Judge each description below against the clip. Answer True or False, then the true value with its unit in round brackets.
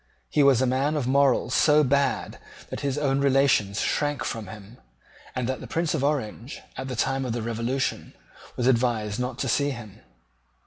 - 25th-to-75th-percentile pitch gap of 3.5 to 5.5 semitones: False (3.1 semitones)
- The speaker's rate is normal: True (185 wpm)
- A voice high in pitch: False (130 Hz)